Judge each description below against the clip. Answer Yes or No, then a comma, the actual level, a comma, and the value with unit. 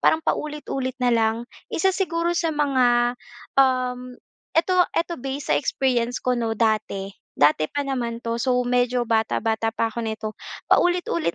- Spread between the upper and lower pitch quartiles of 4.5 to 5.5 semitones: No, average, 3.8 semitones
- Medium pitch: No, very high, 250 Hz